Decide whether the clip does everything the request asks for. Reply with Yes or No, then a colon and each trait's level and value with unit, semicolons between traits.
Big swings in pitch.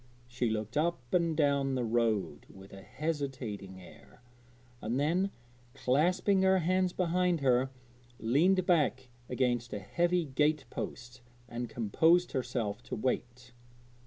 Yes: wide, 6.0 semitones